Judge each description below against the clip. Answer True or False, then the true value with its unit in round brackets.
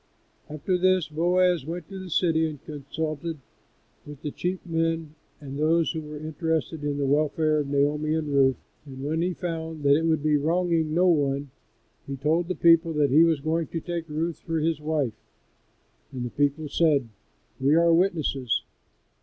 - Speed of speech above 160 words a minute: True (180 wpm)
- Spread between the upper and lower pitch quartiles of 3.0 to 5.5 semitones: False (2.4 semitones)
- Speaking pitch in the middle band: True (155 Hz)